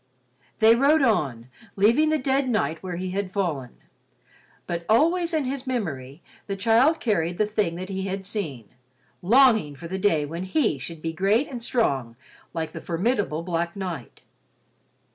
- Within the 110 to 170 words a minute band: Yes, average, 160 wpm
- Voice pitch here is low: No, high, 195 Hz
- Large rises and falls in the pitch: Yes, wide, 6.2 semitones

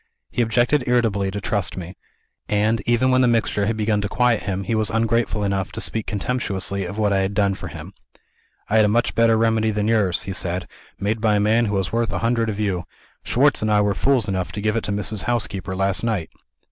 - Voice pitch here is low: Yes, low, 105 Hz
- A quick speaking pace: Yes, fast, 235 wpm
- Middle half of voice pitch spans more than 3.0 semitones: No, narrow, 2.6 semitones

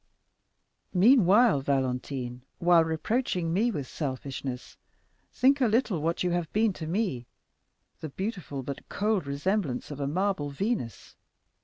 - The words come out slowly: Yes, slow, 125 wpm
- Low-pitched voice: No, medium, 170 Hz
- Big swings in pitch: Yes, wide, 6.9 semitones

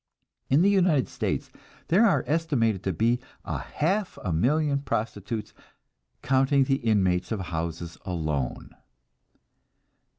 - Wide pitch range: Yes, wide, 8.5 semitones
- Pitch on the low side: Yes, low, 115 Hz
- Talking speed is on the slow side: Yes, slow, 120 wpm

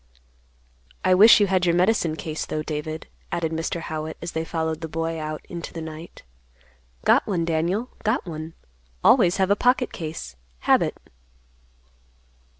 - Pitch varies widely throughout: No, average, 2.7 semitones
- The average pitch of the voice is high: No, medium, 165 Hz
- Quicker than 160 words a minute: No, average, 150 wpm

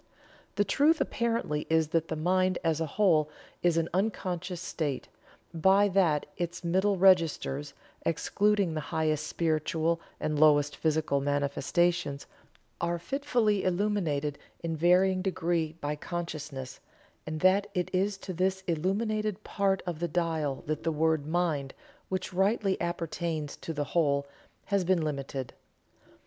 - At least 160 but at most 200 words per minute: No, slow, 135 wpm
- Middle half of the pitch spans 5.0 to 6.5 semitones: No, average, 3.5 semitones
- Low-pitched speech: No, medium, 170 Hz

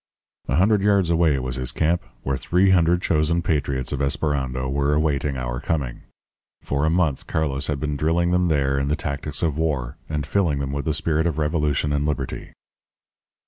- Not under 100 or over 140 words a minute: No, average, 185 wpm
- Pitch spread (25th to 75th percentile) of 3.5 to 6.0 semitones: No, average, 3.1 semitones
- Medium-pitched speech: No, very low, 75 Hz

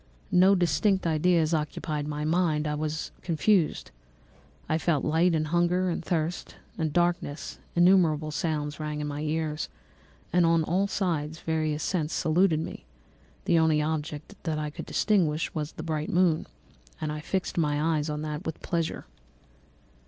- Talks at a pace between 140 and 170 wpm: Yes, average, 155 wpm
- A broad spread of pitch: No, narrow, 2.4 semitones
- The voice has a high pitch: No, medium, 160 Hz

